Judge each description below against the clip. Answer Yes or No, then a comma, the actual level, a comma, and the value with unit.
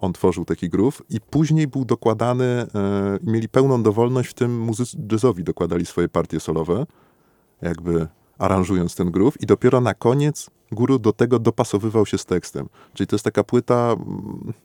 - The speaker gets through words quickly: Yes, fast, 170 wpm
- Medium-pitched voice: No, low, 110 Hz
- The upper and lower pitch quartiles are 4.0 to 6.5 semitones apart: Yes, average, 4.4 semitones